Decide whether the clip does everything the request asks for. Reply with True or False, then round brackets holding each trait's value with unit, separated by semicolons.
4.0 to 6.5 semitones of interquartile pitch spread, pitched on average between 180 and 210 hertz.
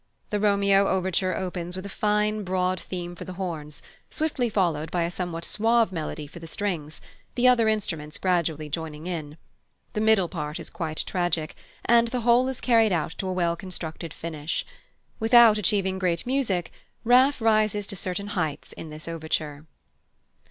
True (4.5 semitones; 185 Hz)